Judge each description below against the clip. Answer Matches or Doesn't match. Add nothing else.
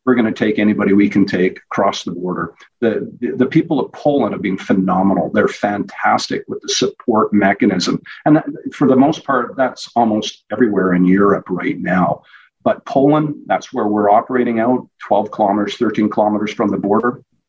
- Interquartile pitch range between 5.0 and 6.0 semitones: Doesn't match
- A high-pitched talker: Doesn't match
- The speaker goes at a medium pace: Matches